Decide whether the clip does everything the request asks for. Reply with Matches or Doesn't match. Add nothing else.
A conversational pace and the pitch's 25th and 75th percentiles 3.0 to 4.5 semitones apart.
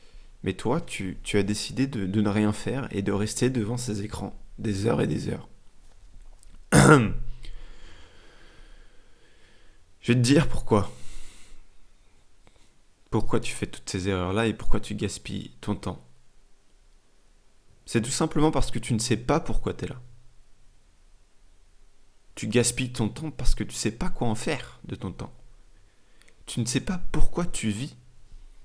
Matches